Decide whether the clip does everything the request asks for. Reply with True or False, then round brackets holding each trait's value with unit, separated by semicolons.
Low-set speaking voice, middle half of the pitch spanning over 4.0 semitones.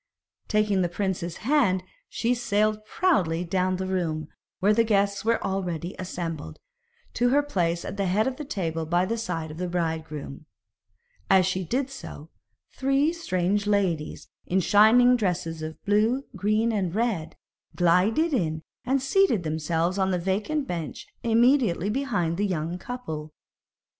False (190 Hz; 5.1 semitones)